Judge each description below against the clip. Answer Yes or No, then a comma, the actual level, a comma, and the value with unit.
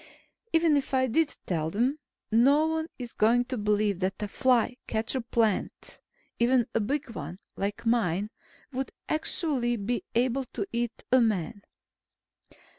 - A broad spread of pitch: No, average, 3.8 semitones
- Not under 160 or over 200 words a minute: No, average, 145 wpm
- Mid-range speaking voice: No, high, 235 Hz